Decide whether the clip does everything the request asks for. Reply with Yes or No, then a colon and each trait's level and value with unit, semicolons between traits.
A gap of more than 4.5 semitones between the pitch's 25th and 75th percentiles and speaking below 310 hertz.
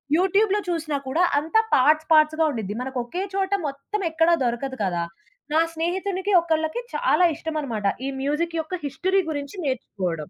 No: average, 4.9 semitones; very high, 315 Hz